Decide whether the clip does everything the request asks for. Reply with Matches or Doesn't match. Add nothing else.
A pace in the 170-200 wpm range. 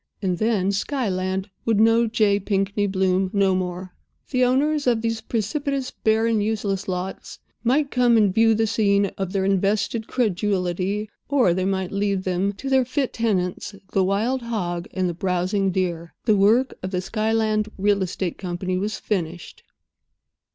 Doesn't match